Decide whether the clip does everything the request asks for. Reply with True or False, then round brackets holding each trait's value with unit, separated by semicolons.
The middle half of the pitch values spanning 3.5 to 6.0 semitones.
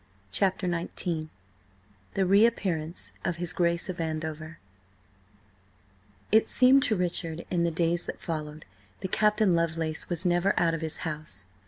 False (2.6 semitones)